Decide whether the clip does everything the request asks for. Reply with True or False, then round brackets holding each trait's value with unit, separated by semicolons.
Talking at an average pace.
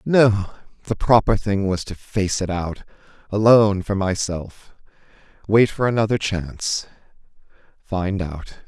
False (105 wpm)